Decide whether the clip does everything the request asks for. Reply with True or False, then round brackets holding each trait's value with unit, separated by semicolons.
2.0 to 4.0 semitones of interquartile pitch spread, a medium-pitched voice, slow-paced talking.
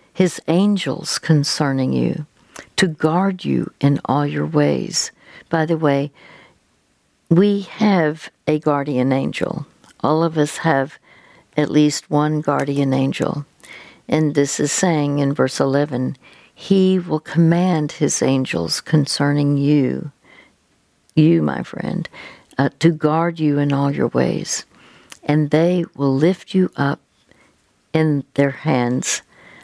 True (2.8 semitones; 150 Hz; 125 wpm)